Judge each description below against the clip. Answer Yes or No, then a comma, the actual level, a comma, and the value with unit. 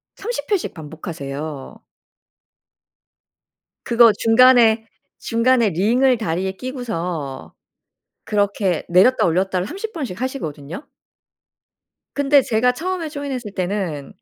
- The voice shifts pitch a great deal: Yes, wide, 6.6 semitones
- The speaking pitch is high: Yes, high, 220 Hz